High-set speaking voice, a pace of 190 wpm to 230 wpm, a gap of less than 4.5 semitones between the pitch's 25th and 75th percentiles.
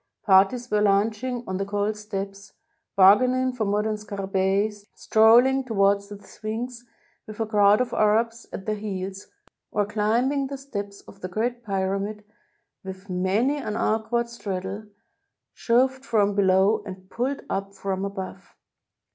No: high, 210 Hz; average, 140 wpm; average, 2.9 semitones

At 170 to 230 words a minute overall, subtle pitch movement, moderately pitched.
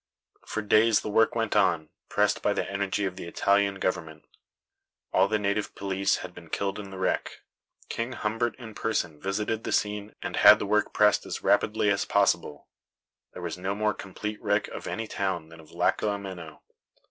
No: average, 185 wpm; narrow, 2.3 semitones; low, 100 Hz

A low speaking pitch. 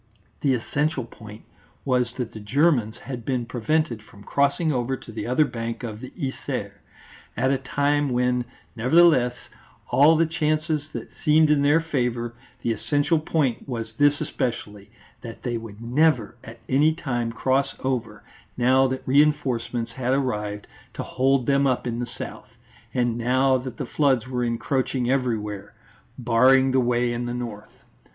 Yes: low, 125 Hz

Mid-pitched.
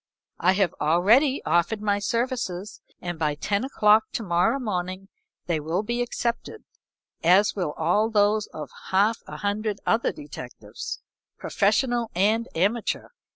No: high, 205 Hz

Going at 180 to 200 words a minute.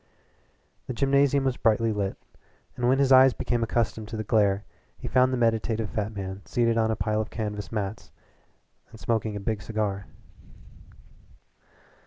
No: average, 155 wpm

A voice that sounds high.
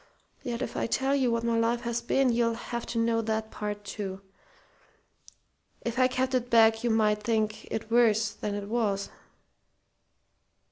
Yes: high, 230 Hz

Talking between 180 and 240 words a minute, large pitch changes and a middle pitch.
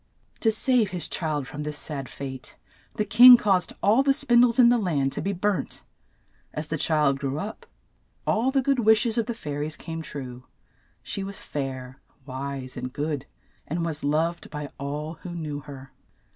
Yes: average, 185 wpm; wide, 7.2 semitones; medium, 155 Hz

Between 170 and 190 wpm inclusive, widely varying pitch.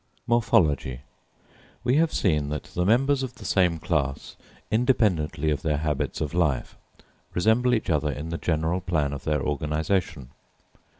No: average, 145 wpm; wide, 6.6 semitones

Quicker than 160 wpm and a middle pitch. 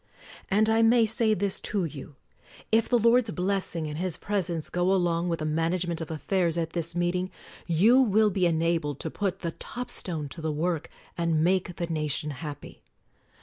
Yes: average, 190 wpm; medium, 175 Hz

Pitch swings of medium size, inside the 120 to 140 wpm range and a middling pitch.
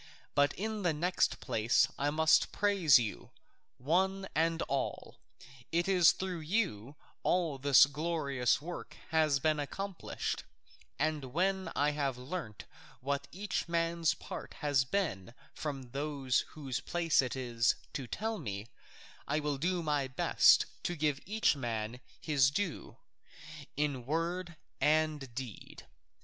Yes: average, 4.3 semitones; slow, 135 wpm; medium, 150 Hz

